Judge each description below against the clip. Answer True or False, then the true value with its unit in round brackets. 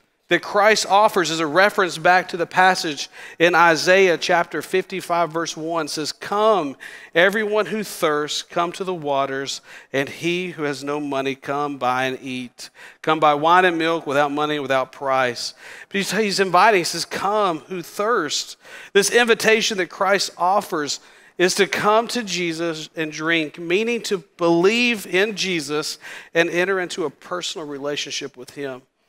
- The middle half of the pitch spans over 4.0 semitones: True (4.7 semitones)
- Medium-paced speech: True (160 wpm)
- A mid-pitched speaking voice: True (170 Hz)